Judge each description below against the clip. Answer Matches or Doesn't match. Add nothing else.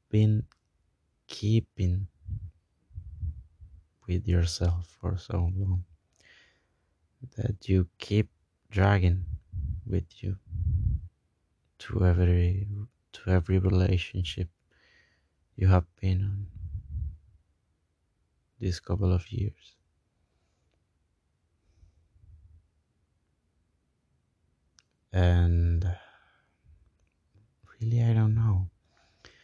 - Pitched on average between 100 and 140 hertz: Doesn't match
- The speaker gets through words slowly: Matches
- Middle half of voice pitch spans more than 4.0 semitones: Doesn't match